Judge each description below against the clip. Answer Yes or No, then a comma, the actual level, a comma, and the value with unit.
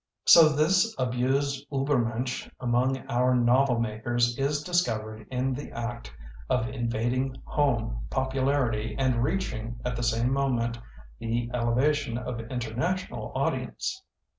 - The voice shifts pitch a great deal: No, average, 2.7 semitones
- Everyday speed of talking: No, slow, 120 wpm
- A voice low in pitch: Yes, low, 125 Hz